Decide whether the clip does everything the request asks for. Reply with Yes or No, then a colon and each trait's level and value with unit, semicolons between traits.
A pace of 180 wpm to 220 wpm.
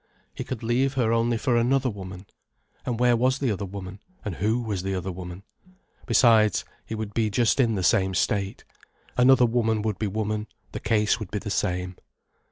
Yes: average, 190 wpm